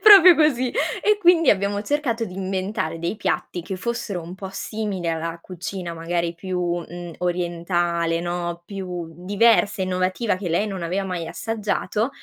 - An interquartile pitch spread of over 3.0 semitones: Yes, average, 3.6 semitones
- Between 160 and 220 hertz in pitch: Yes, medium, 185 Hz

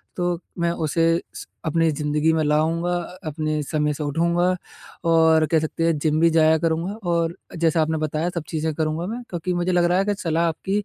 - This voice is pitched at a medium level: Yes, medium, 165 Hz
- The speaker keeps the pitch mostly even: Yes, narrow, 1.7 semitones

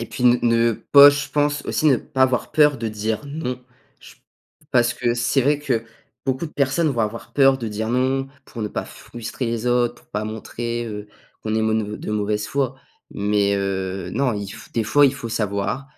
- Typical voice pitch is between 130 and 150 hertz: No, low, 120 Hz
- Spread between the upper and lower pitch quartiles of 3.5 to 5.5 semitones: Yes, average, 3.9 semitones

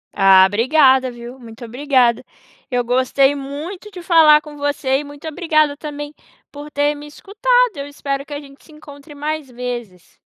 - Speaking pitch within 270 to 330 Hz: Yes, very high, 285 Hz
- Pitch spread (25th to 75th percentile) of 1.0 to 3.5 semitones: Yes, average, 2.9 semitones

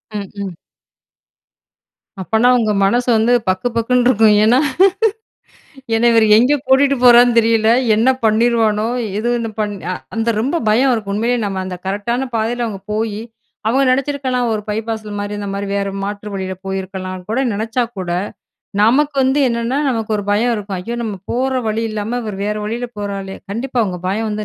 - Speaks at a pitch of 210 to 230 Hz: Yes, high, 220 Hz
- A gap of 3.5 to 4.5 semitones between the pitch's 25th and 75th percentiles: No, average, 3.0 semitones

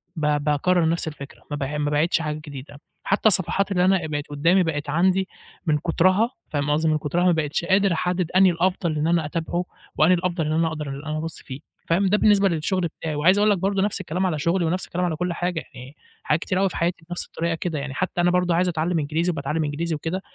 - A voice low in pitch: No, medium, 170 Hz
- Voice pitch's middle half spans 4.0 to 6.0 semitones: No, average, 3.1 semitones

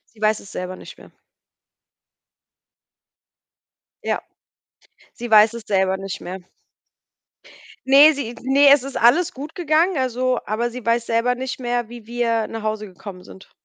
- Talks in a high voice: Yes, high, 235 Hz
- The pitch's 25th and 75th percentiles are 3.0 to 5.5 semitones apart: Yes, average, 3.5 semitones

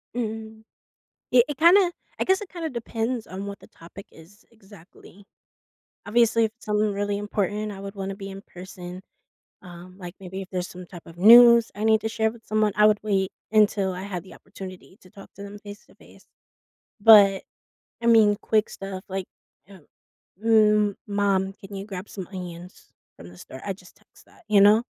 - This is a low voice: No, high, 205 Hz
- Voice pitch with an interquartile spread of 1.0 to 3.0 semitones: Yes, narrow, 2.5 semitones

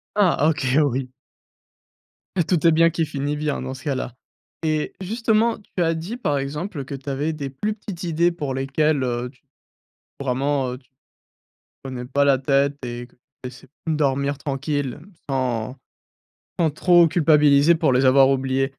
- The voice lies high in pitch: No, medium, 140 Hz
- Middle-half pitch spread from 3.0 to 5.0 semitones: Yes, average, 3.3 semitones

